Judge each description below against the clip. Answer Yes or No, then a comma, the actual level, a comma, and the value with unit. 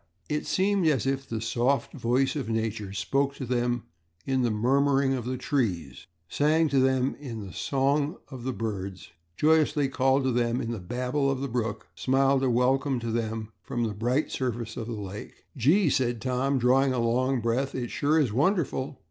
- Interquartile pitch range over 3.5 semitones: No, average, 2.9 semitones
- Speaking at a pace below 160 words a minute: No, average, 190 wpm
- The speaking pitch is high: No, low, 130 Hz